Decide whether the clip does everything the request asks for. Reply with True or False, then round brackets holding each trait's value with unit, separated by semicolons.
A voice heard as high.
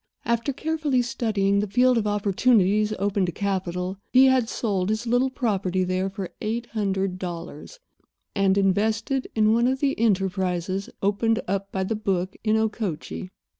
True (205 Hz)